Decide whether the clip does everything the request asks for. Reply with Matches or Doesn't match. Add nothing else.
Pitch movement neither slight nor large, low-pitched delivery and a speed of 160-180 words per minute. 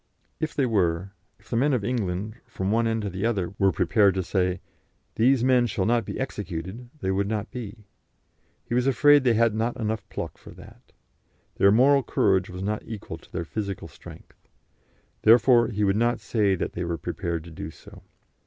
Doesn't match